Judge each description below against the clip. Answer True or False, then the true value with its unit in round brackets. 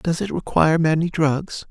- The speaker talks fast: False (175 wpm)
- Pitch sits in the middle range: True (155 Hz)